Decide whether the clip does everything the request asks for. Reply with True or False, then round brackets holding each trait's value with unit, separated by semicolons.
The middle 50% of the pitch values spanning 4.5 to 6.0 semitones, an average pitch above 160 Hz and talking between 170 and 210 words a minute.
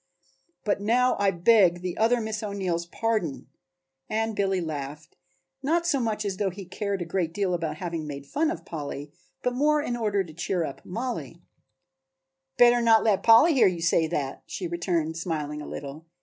True (5.4 semitones; 190 Hz; 180 wpm)